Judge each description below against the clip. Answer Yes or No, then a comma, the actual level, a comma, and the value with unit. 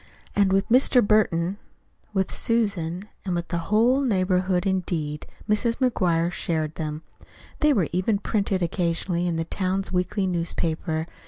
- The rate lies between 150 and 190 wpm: No, slow, 135 wpm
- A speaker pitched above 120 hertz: Yes, medium, 185 Hz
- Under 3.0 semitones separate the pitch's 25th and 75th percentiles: No, average, 3.5 semitones